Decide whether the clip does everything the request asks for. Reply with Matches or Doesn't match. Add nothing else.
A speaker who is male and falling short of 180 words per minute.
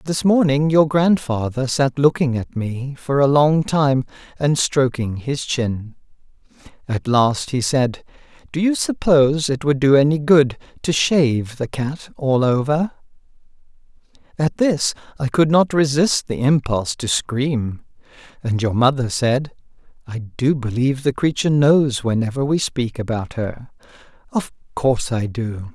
Matches